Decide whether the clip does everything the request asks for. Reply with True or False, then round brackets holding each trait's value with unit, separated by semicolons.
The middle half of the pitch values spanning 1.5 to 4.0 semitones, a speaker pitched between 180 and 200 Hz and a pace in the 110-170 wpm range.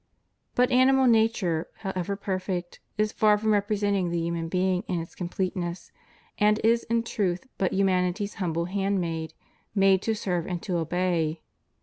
True (3.1 semitones; 190 Hz; 145 wpm)